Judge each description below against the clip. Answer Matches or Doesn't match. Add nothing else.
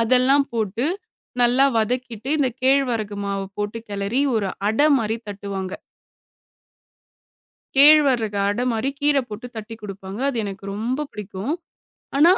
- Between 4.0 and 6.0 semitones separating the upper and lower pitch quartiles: Matches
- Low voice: Doesn't match